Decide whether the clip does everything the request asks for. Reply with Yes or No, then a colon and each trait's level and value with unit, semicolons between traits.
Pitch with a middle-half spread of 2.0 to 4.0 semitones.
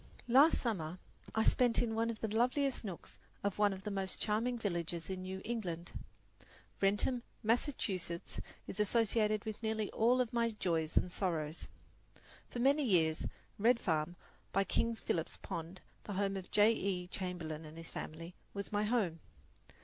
No: average, 4.5 semitones